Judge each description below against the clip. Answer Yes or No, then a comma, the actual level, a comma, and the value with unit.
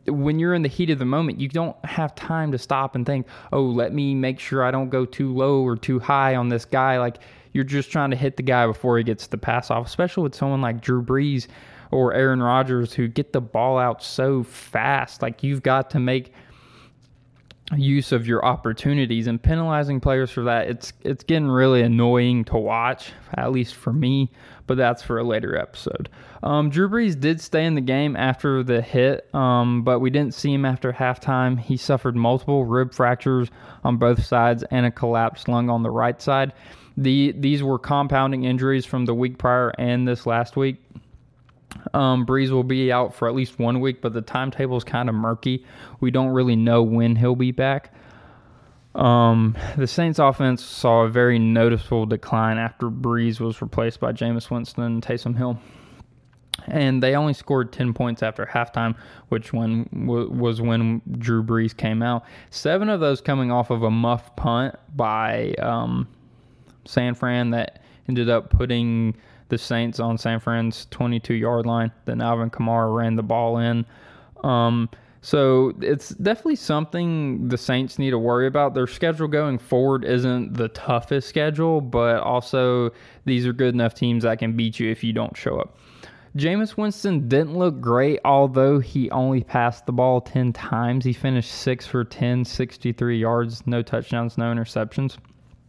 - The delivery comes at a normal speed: Yes, average, 185 wpm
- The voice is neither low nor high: No, low, 125 Hz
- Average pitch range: No, narrow, 2.3 semitones